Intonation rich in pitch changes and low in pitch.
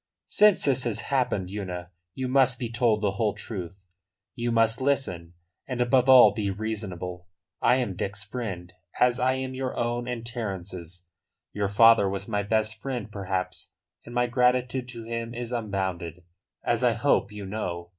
No: average, 4.1 semitones; low, 110 Hz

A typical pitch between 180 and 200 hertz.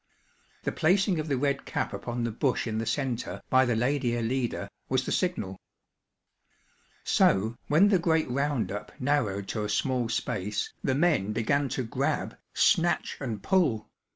No: low, 130 Hz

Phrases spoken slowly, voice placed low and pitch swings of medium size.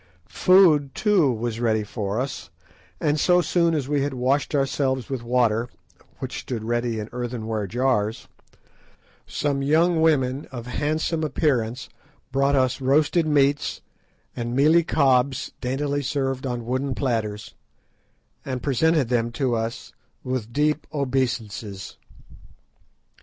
Yes: slow, 125 wpm; low, 130 Hz; average, 3.6 semitones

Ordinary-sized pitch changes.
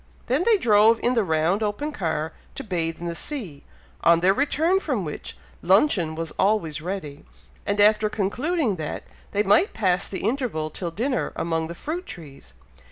No: wide, 6.8 semitones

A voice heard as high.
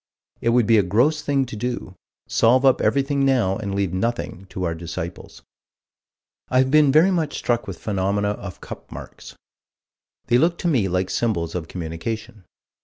No: low, 110 Hz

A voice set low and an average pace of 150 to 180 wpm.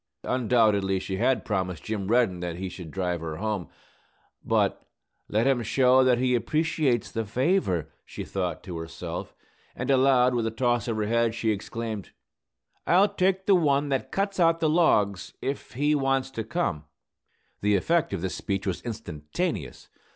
Yes: low, 115 Hz; average, 165 wpm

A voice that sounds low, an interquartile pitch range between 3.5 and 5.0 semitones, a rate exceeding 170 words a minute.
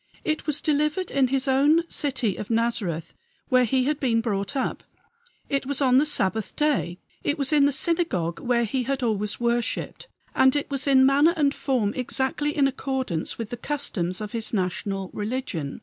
No: very high, 260 Hz; average, 4.6 semitones; average, 180 wpm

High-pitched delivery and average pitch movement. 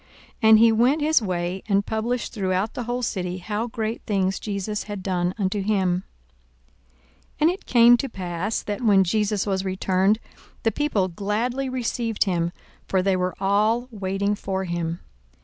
Yes: high, 205 Hz; average, 3.4 semitones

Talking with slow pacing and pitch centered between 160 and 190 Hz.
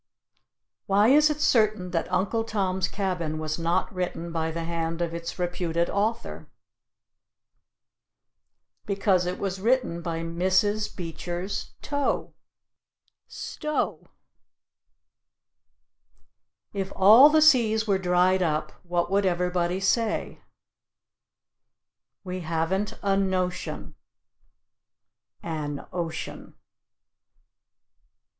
Yes: slow, 95 wpm; medium, 185 Hz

